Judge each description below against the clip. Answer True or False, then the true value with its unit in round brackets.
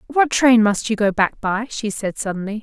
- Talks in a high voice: True (220 Hz)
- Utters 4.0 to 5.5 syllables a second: True (5.0 syllables/s)